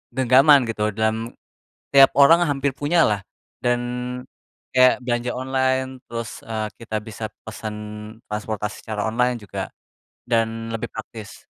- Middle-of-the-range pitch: No, low, 115 Hz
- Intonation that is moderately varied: Yes, average, 3.0 semitones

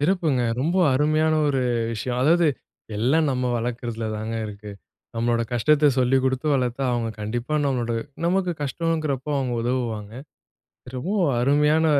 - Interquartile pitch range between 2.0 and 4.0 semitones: No, average, 4.4 semitones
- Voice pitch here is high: No, low, 130 Hz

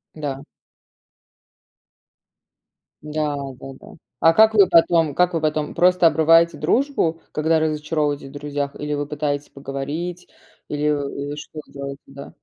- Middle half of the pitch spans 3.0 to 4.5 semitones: No, narrow, 2.4 semitones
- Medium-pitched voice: Yes, medium, 150 Hz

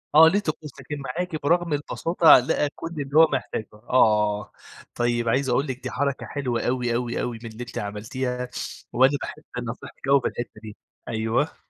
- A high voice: No, low, 130 Hz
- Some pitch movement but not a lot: Yes, average, 3.6 semitones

